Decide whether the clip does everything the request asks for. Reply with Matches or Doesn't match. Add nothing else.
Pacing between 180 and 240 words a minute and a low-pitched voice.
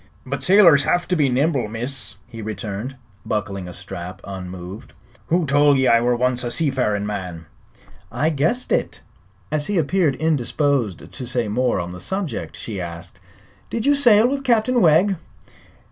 Doesn't match